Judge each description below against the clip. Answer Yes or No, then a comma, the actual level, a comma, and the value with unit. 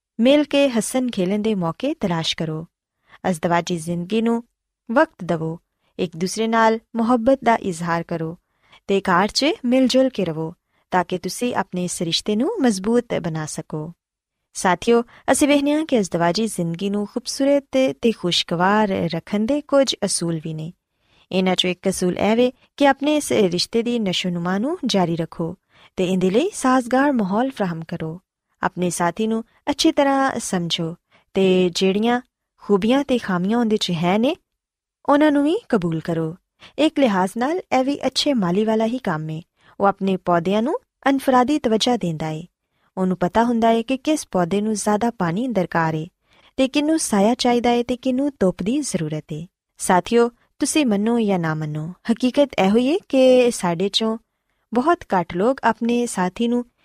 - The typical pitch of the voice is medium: No, high, 215 Hz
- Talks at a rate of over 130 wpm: Yes, average, 160 wpm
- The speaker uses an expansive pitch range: Yes, wide, 6.0 semitones